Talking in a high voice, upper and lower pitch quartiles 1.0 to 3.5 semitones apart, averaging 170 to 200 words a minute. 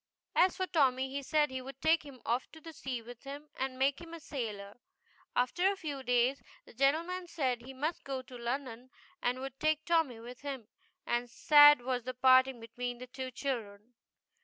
Yes: very high, 265 Hz; average, 3.1 semitones; average, 190 wpm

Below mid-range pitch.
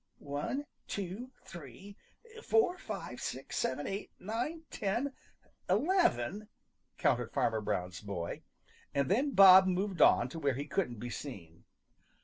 No: medium, 180 Hz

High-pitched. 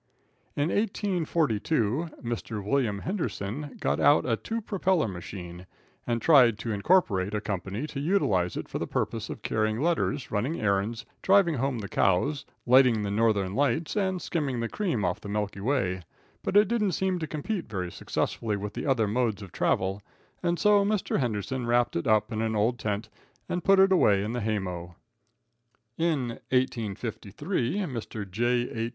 No: low, 120 Hz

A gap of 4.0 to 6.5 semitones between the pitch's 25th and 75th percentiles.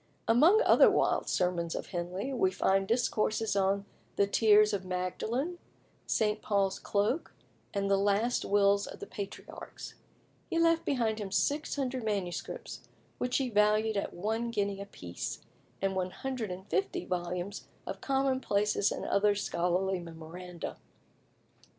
No: average, 3.5 semitones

